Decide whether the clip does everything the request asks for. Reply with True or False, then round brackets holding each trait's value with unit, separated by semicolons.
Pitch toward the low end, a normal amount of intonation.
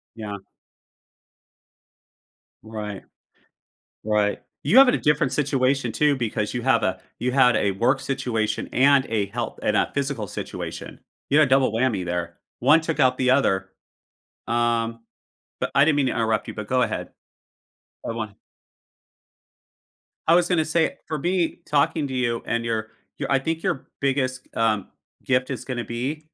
True (125 Hz; 4.0 semitones)